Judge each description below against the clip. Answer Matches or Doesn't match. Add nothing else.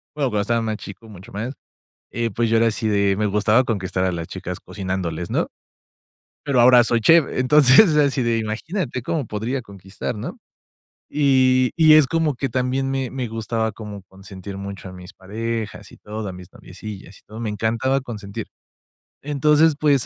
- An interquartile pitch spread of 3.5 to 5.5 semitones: Matches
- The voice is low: Matches